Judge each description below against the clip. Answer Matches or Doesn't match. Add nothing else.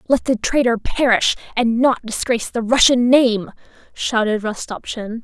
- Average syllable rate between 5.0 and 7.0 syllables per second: Doesn't match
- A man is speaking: Doesn't match